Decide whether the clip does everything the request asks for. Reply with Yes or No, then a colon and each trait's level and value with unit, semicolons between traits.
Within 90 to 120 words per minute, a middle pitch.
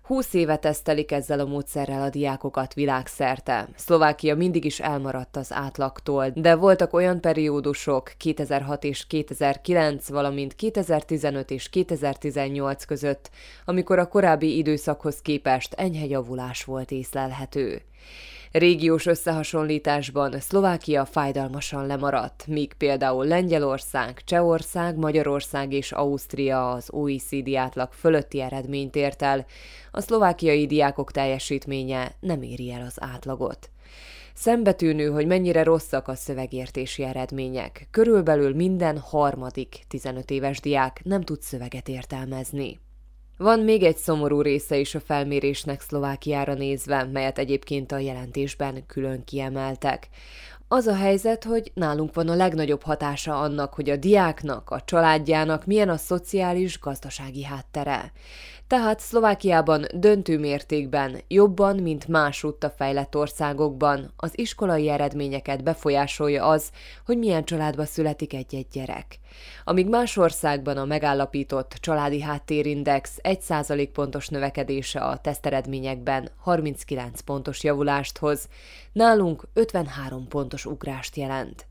Yes: average, 115 wpm; medium, 145 Hz